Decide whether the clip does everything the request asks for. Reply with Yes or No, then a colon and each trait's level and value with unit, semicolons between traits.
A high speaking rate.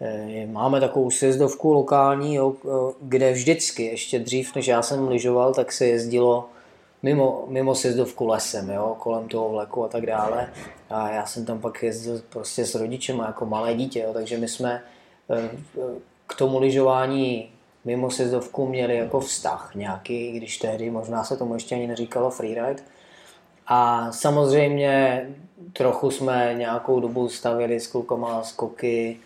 No: average, 150 wpm